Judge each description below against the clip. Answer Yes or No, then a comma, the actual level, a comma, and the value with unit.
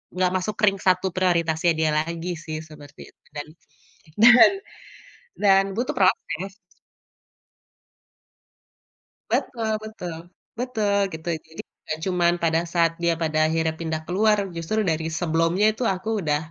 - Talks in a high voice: No, medium, 170 Hz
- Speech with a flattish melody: No, average, 3.2 semitones